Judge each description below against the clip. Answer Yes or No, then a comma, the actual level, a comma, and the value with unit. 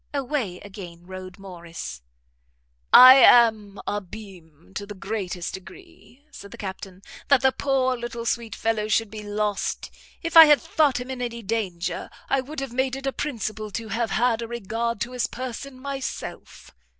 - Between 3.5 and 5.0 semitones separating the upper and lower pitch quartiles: Yes, average, 4.6 semitones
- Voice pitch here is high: Yes, high, 225 Hz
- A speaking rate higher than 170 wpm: No, average, 165 wpm